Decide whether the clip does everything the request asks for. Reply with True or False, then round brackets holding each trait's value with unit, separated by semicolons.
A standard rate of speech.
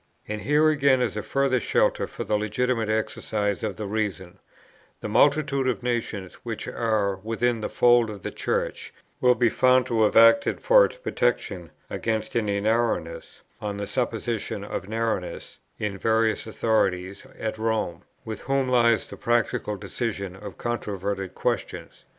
True (155 wpm)